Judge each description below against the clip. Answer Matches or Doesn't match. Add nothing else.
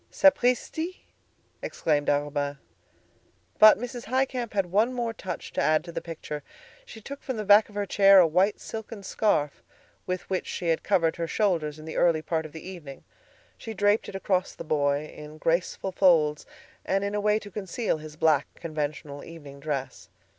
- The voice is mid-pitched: Matches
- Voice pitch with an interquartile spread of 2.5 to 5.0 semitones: Doesn't match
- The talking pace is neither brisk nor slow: Matches